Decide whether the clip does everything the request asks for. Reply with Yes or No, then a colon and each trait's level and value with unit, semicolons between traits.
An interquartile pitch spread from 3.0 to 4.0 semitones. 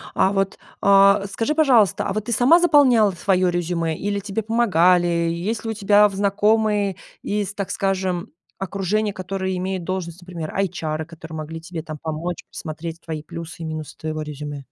Yes: average, 3.7 semitones